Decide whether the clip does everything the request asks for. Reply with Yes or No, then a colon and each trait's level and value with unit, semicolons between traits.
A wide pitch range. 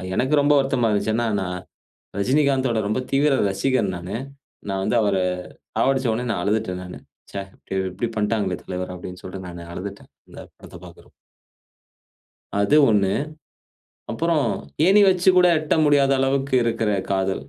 Yes: wide, 6.0 semitones